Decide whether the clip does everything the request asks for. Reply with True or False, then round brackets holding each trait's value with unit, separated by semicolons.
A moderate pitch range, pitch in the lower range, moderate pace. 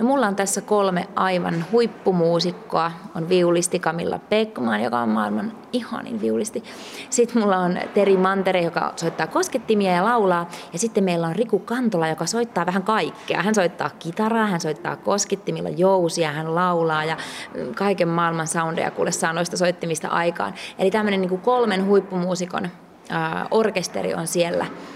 False (4.3 semitones; 185 Hz; 145 wpm)